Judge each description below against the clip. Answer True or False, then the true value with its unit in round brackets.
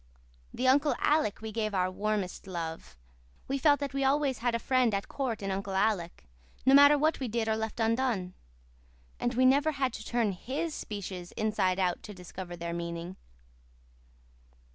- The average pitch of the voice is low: False (220 Hz)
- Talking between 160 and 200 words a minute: True (175 wpm)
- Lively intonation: True (6.0 semitones)